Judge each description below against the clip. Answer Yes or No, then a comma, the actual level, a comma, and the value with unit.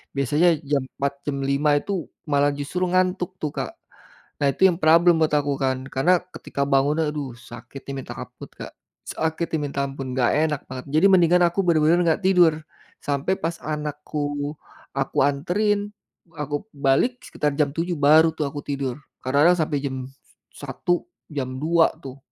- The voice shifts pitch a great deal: No, average, 3.6 semitones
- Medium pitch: Yes, medium, 150 Hz